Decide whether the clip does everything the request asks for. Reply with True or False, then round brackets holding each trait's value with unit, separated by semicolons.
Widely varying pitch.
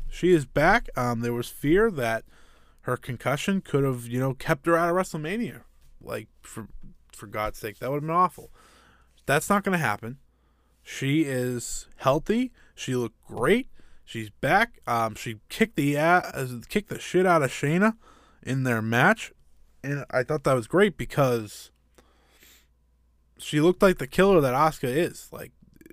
True (6.4 semitones)